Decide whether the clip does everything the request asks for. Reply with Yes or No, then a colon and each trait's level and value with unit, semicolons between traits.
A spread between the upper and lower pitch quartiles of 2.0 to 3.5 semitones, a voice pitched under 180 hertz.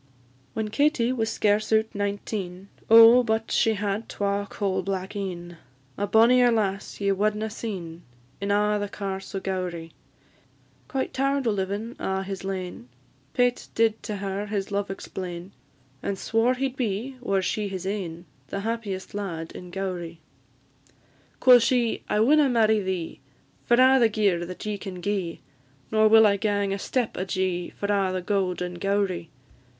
No: average, 2.8 semitones; high, 200 Hz